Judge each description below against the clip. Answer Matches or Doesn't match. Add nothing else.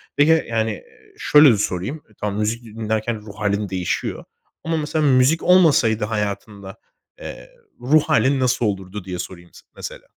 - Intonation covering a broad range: Matches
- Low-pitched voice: Matches